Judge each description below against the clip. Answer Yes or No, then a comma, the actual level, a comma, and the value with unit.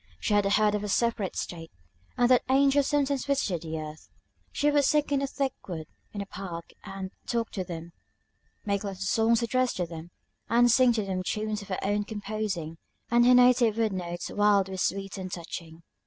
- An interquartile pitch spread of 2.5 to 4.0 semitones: No, average, 4.6 semitones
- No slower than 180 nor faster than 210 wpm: Yes, average, 200 wpm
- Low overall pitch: No, high, 205 Hz